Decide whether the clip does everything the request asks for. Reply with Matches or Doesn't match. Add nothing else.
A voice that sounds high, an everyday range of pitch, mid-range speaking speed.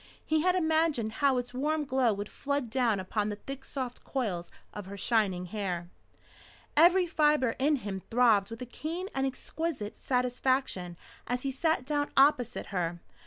Doesn't match